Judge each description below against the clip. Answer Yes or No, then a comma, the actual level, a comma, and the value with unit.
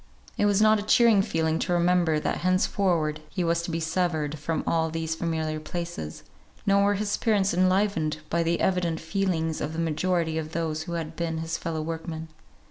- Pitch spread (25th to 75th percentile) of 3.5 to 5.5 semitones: No, narrow, 2.4 semitones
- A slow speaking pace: No, average, 190 wpm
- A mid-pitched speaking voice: Yes, medium, 165 Hz